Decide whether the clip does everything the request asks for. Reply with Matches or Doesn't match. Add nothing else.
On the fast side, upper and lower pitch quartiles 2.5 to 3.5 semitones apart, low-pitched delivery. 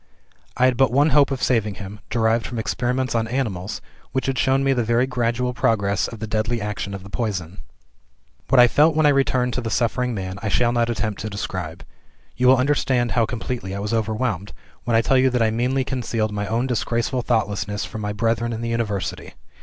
Matches